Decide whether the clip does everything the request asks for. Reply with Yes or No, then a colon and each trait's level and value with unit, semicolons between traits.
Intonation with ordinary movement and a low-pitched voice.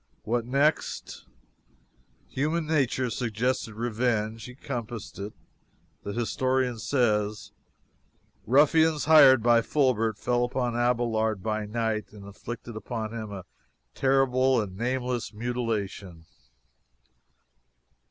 Yes: average, 3.0 semitones; low, 120 Hz